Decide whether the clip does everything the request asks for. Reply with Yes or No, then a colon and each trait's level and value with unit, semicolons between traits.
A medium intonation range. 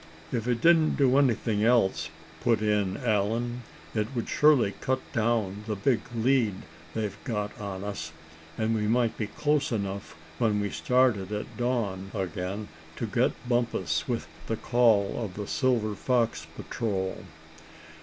Yes: average, 3.2 semitones